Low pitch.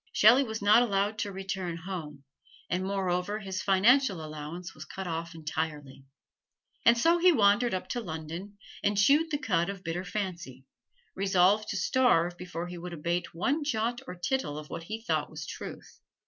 No: high, 190 Hz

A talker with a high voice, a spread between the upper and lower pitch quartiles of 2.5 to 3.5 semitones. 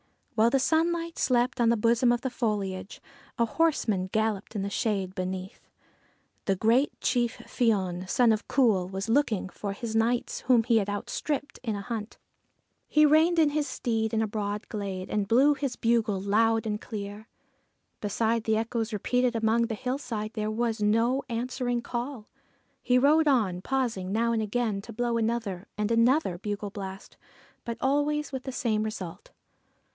Yes: high, 225 Hz; average, 3.1 semitones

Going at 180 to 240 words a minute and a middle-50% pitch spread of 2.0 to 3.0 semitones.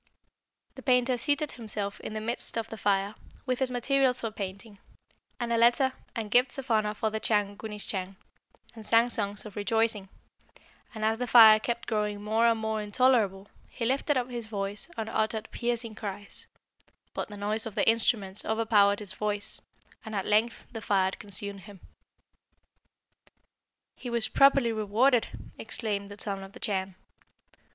No: average, 165 wpm; narrow, 2.5 semitones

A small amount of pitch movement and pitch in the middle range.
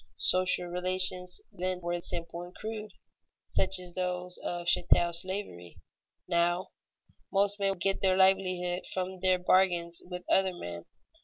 Yes: narrow, 1.3 semitones; medium, 180 Hz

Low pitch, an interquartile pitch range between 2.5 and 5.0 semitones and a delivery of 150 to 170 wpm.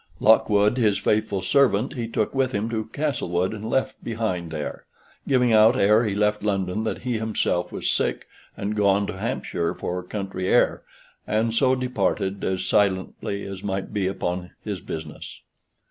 Yes: low, 105 Hz; average, 2.9 semitones; average, 160 wpm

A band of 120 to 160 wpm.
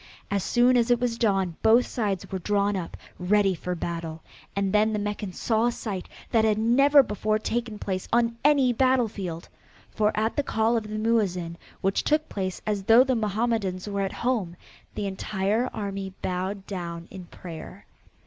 No: average, 175 wpm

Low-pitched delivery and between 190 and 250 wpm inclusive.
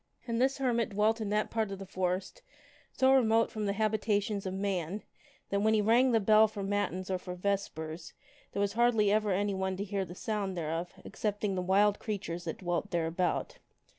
No: high, 200 Hz; average, 195 wpm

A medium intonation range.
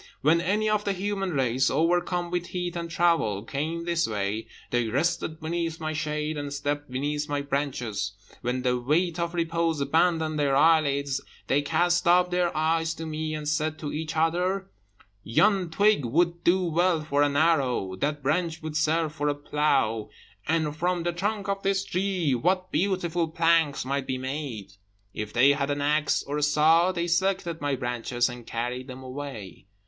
Yes: average, 3.7 semitones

